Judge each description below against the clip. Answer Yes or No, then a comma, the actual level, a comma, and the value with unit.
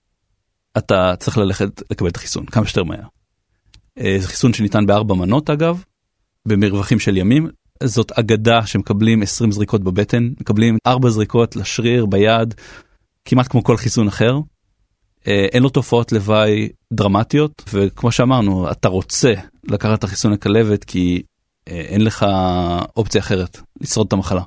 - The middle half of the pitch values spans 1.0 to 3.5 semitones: Yes, average, 2.7 semitones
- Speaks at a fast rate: No, average, 135 wpm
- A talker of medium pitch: No, low, 105 Hz